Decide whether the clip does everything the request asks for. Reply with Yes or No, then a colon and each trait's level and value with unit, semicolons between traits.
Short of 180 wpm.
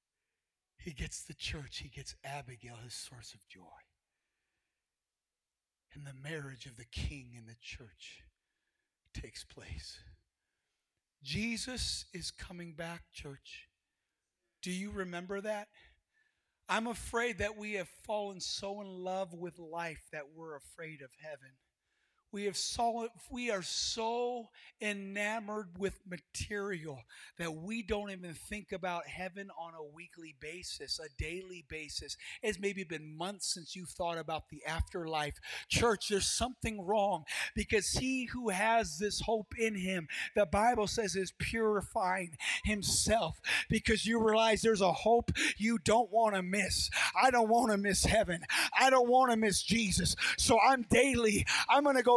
Yes: average, 145 wpm